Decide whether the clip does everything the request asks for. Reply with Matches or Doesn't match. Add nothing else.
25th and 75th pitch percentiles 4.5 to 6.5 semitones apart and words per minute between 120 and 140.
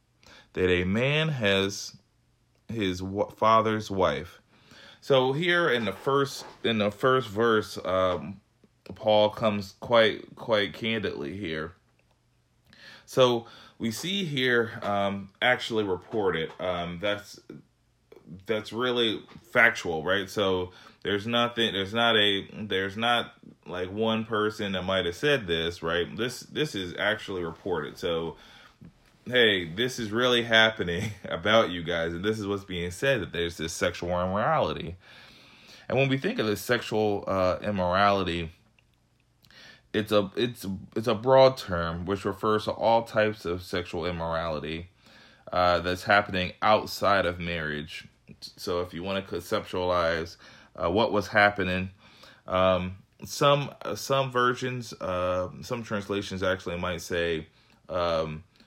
Doesn't match